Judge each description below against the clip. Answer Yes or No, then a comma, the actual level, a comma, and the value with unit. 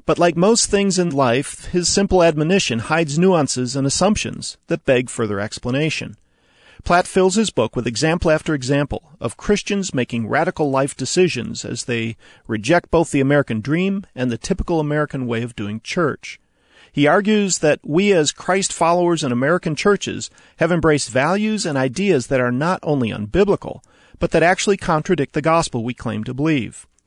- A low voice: No, medium, 155 Hz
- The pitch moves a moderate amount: No, wide, 6.2 semitones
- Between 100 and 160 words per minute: No, average, 170 wpm